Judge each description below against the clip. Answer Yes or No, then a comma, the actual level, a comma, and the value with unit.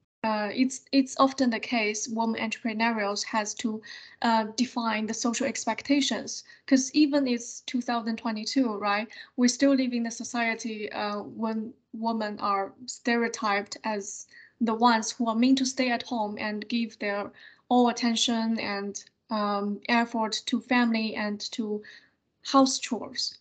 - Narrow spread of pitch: Yes, narrow, 2.2 semitones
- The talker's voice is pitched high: Yes, high, 230 Hz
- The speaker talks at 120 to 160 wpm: Yes, average, 140 wpm